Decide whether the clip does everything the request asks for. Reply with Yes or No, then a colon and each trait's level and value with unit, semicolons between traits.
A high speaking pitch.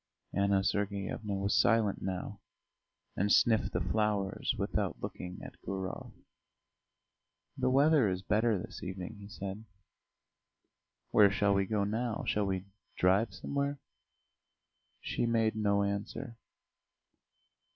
No: low, 100 Hz